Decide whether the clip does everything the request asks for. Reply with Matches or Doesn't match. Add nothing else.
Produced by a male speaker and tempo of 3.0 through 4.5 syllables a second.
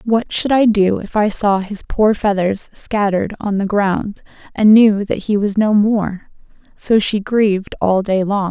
Doesn't match